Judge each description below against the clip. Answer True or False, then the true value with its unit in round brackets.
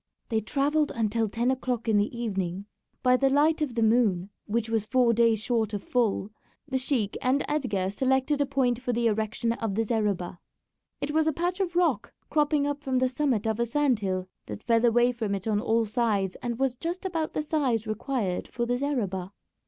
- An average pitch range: True (4.1 semitones)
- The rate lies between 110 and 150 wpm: False (205 wpm)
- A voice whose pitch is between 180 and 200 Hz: False (235 Hz)